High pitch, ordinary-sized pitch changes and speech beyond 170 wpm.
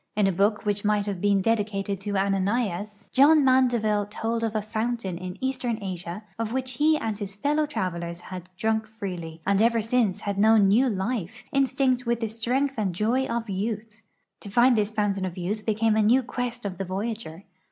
Yes: high, 215 Hz; average, 3.2 semitones; average, 195 wpm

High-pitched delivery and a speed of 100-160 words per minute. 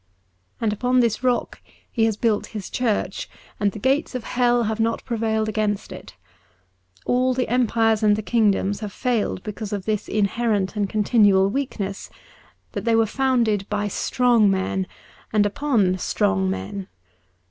Yes: high, 215 Hz; average, 155 wpm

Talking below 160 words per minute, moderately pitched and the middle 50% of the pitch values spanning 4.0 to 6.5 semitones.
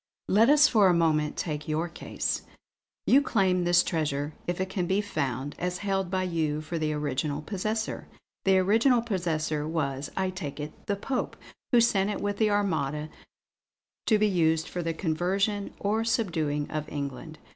No: average, 170 wpm; medium, 175 Hz; average, 4.8 semitones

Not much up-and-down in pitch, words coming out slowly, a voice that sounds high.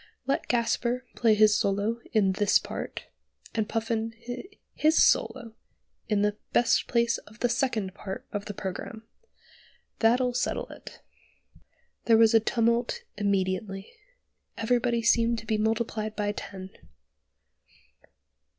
Yes: narrow, 2.2 semitones; slow, 125 wpm; high, 225 Hz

